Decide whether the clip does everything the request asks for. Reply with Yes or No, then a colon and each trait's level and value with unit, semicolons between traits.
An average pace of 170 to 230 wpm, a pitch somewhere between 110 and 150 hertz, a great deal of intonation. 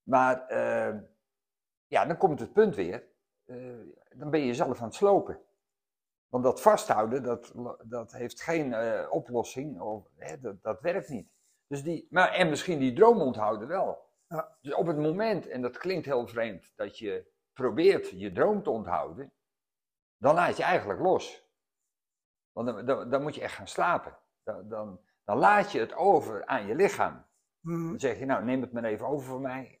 Yes: average, 185 wpm; medium, 140 Hz; wide, 7.6 semitones